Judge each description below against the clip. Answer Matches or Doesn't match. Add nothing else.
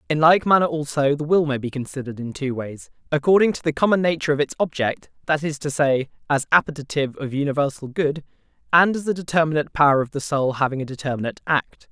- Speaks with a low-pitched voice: Doesn't match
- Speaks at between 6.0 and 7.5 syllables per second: Matches